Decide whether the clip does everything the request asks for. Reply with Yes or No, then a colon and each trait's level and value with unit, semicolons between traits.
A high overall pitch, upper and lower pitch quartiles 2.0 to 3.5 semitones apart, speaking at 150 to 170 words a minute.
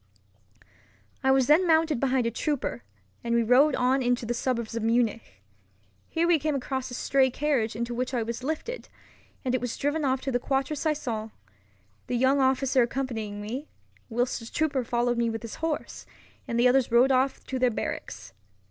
No: very high, 250 Hz; average, 2.7 semitones; average, 180 wpm